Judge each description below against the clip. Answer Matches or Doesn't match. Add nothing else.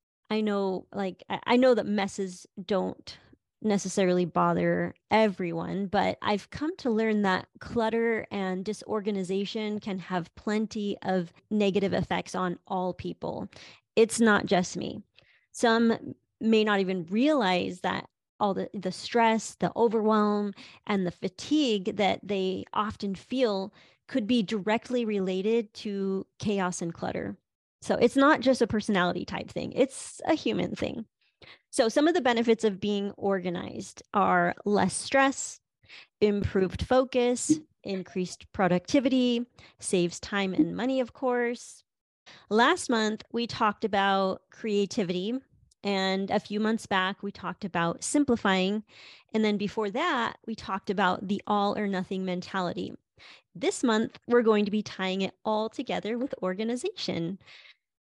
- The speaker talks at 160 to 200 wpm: Doesn't match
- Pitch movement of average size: Matches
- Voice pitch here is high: Matches